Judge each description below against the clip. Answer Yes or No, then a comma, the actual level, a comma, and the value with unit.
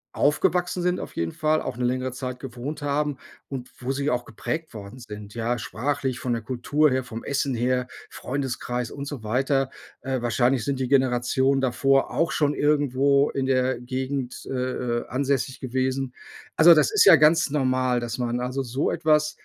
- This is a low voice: Yes, low, 130 Hz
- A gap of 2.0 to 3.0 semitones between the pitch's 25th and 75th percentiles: Yes, narrow, 2.4 semitones